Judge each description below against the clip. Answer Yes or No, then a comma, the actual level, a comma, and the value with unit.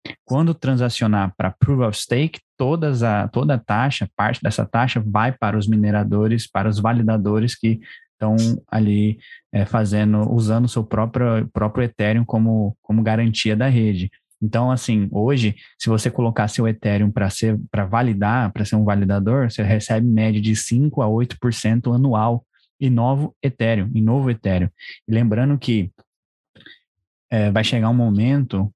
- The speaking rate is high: No, average, 150 wpm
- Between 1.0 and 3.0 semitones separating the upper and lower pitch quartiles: Yes, narrow, 2.4 semitones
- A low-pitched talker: Yes, low, 110 Hz